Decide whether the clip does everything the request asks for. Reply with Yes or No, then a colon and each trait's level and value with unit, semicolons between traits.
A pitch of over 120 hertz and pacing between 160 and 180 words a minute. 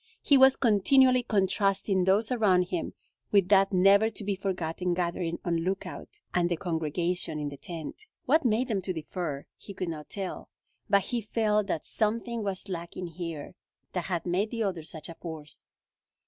Yes: high, 190 Hz; average, 175 wpm